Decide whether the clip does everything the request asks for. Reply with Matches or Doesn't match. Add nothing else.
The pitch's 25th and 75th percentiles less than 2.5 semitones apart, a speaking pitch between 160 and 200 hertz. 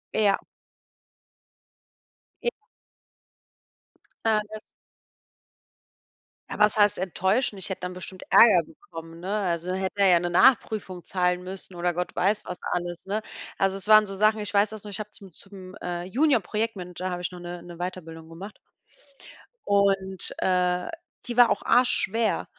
Doesn't match